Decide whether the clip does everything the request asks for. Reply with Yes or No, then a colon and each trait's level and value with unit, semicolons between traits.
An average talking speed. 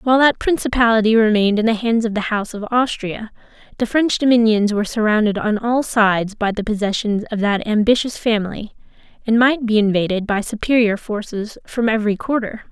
Yes: average, 175 wpm